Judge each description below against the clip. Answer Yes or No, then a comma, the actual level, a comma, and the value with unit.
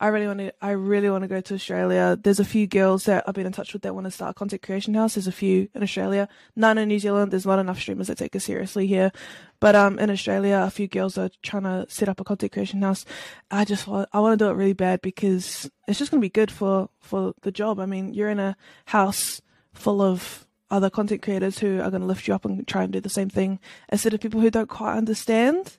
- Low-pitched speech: No, high, 195 Hz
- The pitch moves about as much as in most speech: No, narrow, 1.7 semitones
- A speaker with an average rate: No, fast, 270 wpm